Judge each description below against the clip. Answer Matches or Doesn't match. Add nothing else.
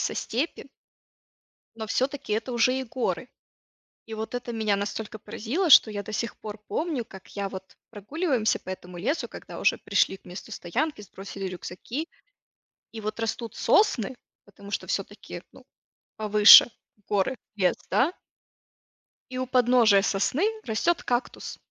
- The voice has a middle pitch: Doesn't match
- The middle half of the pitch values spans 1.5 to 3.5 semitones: Doesn't match